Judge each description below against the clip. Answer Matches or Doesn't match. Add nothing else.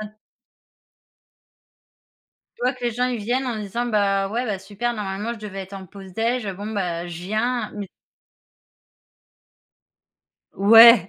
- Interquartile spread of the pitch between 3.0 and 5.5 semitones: Matches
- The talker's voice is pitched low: Doesn't match